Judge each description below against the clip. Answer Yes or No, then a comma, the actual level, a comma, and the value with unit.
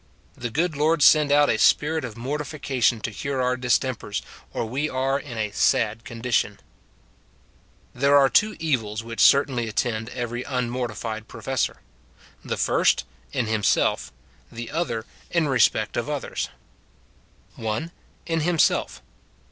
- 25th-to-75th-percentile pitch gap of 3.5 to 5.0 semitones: Yes, average, 4.0 semitones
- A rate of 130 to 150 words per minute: Yes, average, 140 wpm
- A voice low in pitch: Yes, low, 125 Hz